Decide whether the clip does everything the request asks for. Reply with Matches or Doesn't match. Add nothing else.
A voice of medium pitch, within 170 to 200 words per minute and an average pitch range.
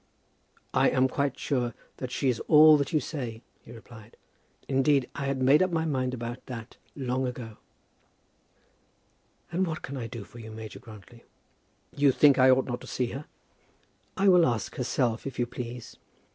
Doesn't match